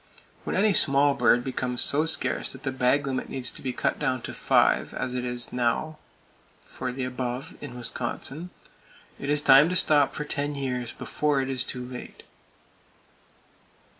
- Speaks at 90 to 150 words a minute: No, average, 170 wpm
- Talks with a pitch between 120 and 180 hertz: Yes, low, 135 Hz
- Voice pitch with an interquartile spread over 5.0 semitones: No, narrow, 2.6 semitones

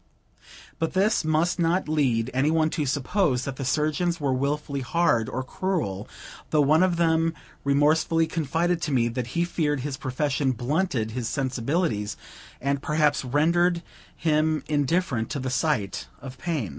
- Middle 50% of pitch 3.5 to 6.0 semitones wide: Yes, average, 4.0 semitones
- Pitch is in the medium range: Yes, medium, 150 Hz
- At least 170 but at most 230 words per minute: No, average, 155 wpm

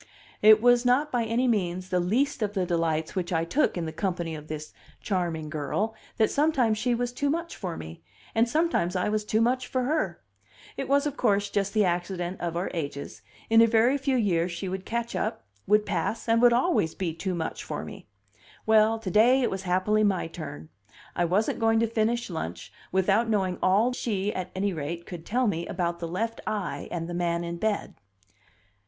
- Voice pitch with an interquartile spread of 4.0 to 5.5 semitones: Yes, average, 5.0 semitones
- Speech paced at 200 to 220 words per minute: Yes, fast, 205 wpm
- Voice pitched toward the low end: No, high, 200 Hz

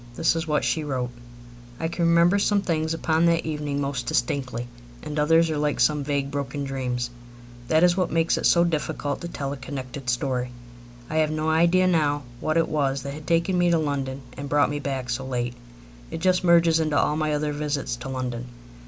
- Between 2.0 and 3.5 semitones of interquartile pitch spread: Yes, average, 3.2 semitones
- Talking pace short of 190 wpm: No, fast, 205 wpm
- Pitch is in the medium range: Yes, medium, 150 Hz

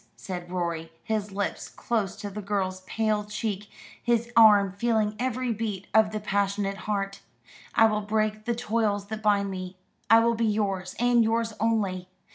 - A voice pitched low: No, high, 210 Hz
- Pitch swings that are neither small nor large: No, narrow, 2.2 semitones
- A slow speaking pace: No, average, 165 wpm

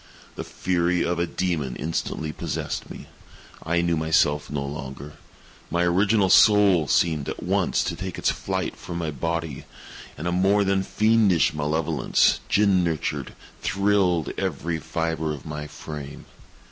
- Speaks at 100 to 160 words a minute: Yes, average, 145 wpm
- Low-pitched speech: Yes, very low, 85 Hz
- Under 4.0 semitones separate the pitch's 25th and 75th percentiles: Yes, average, 3.5 semitones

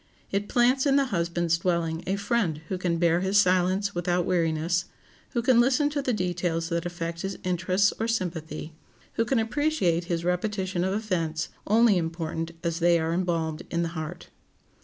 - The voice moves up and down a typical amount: Yes, average, 3.5 semitones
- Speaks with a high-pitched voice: No, medium, 180 Hz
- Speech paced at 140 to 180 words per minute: Yes, average, 175 wpm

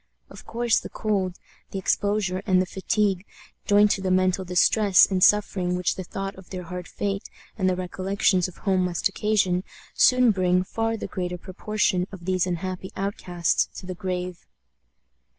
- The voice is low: No, medium, 185 Hz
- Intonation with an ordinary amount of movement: No, narrow, 1.9 semitones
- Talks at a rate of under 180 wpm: Yes, average, 170 wpm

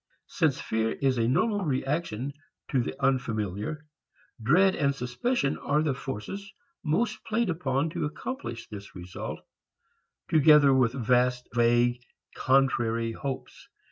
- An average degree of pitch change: Yes, average, 4.6 semitones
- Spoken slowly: Yes, slow, 120 wpm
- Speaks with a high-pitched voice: No, low, 135 Hz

